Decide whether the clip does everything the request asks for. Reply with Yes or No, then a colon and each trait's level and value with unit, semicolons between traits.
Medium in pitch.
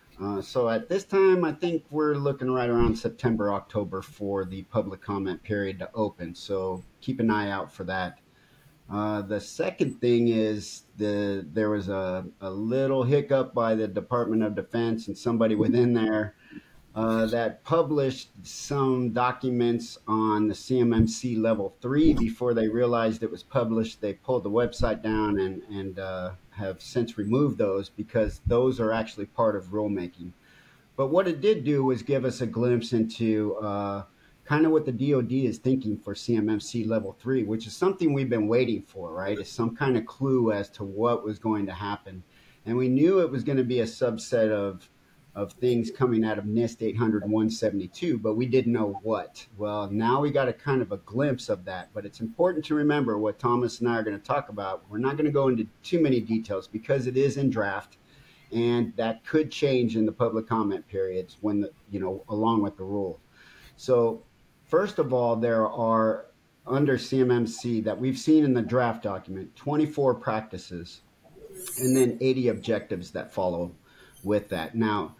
No: low, 115 Hz